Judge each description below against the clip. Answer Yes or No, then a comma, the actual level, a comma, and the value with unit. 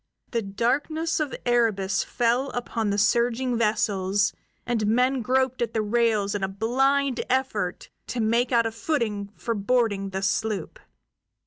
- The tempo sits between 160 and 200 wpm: No, average, 145 wpm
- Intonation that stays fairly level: No, average, 3.4 semitones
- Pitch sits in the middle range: No, high, 230 Hz